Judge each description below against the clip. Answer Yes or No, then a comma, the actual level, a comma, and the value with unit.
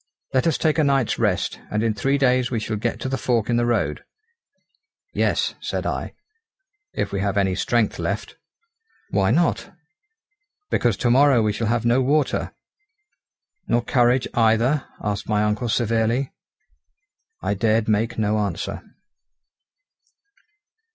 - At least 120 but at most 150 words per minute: Yes, average, 145 wpm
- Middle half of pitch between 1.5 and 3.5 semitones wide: Yes, average, 3.2 semitones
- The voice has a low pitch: Yes, low, 115 Hz